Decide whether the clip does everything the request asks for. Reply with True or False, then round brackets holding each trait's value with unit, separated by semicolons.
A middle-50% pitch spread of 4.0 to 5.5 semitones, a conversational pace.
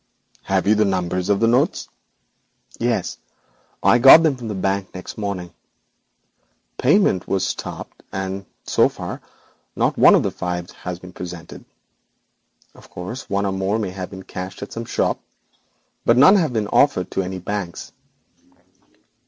False (3.3 semitones; 160 wpm)